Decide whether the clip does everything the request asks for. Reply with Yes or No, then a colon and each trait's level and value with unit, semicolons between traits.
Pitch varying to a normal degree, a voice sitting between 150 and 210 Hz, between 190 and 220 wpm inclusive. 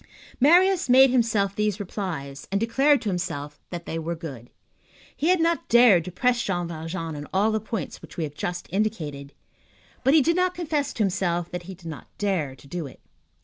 No: wide, 7.0 semitones; high, 190 Hz; average, 200 wpm